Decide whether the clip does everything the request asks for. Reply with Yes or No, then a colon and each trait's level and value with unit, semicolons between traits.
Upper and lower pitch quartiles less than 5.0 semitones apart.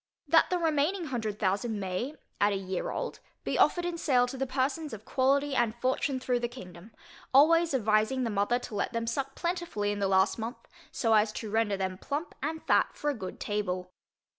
No: average, 5.3 semitones